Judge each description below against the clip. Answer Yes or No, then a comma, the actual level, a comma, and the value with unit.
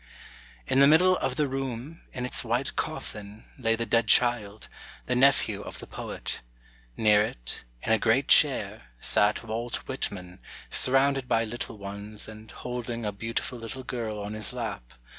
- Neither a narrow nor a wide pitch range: Yes, average, 3.1 semitones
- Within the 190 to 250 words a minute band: No, average, 160 wpm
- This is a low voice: Yes, low, 115 Hz